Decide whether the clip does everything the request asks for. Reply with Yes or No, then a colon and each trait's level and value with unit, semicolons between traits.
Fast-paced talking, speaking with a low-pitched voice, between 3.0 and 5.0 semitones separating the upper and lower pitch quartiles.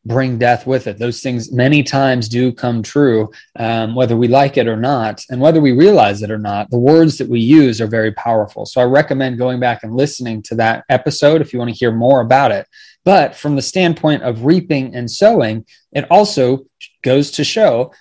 Yes: fast, 215 wpm; low, 125 Hz; average, 3.3 semitones